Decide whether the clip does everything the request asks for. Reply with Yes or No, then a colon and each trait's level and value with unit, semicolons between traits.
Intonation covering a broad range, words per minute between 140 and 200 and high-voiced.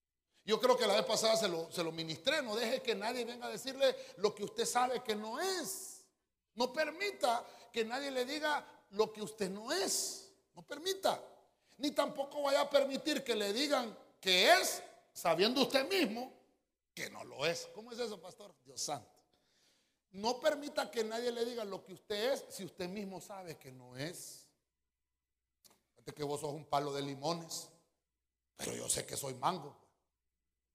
Yes: wide, 8.4 semitones; average, 180 wpm; high, 220 Hz